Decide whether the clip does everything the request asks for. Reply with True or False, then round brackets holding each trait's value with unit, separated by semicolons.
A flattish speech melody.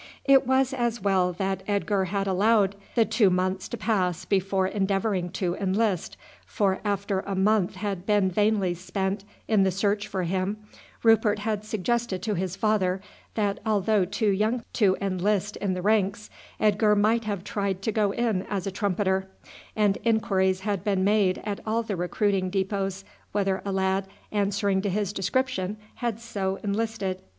True (2.1 semitones)